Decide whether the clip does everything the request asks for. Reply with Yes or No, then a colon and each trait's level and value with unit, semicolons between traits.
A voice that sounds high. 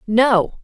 Yes: high, 225 Hz